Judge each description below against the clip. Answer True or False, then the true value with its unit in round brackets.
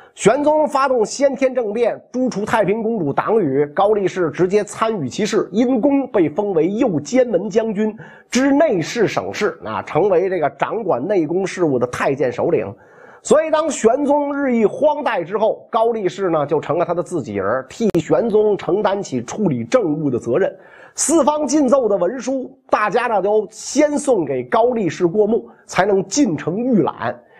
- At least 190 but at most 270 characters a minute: True (260 characters per minute)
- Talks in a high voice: True (225 Hz)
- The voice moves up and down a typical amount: False (6.1 semitones)